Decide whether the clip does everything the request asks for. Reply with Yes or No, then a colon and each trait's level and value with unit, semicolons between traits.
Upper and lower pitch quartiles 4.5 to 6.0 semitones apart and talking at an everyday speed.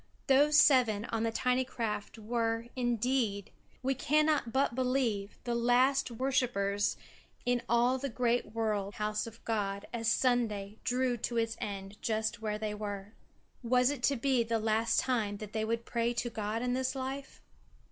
No: average, 2.9 semitones; average, 165 wpm